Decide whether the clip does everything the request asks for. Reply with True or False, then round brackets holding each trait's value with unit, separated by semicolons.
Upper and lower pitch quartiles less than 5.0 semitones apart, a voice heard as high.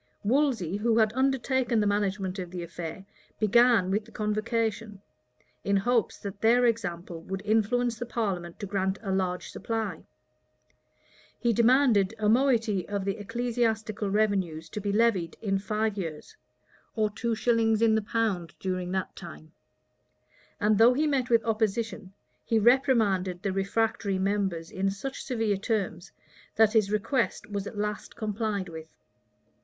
True (3.0 semitones; 210 Hz)